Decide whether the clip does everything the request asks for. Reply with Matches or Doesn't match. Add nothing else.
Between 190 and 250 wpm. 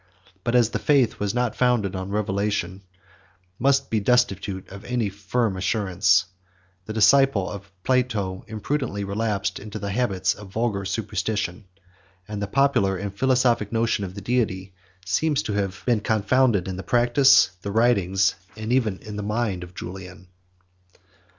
Doesn't match